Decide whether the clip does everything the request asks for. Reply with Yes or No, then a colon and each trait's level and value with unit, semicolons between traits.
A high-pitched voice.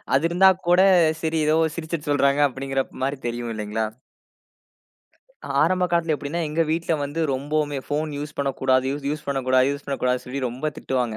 No: medium, 140 Hz